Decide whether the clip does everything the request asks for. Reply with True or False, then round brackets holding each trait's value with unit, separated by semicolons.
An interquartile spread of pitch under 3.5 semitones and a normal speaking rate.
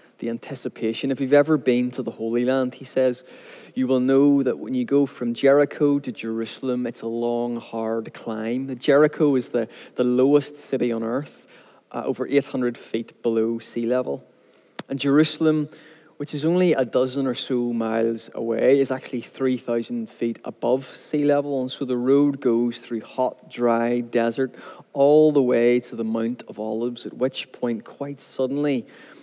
True (3.1 semitones; 170 wpm)